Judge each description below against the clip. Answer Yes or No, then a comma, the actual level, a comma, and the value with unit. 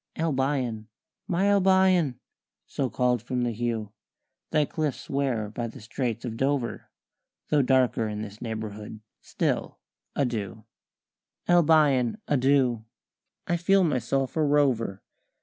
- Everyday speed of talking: No, slow, 115 wpm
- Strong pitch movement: No, average, 4.6 semitones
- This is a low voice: Yes, low, 130 Hz